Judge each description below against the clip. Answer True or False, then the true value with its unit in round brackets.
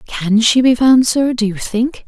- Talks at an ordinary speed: False (230 wpm)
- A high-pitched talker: True (235 Hz)